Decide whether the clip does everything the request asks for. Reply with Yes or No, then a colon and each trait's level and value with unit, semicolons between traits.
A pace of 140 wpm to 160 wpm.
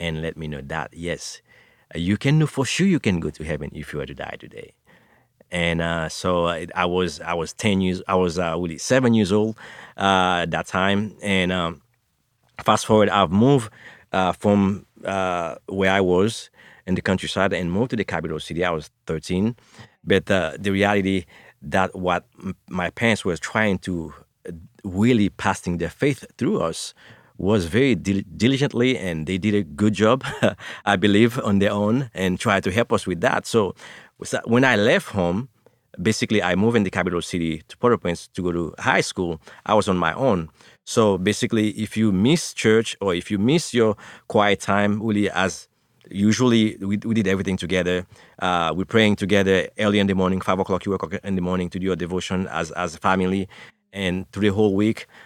No: average, 195 wpm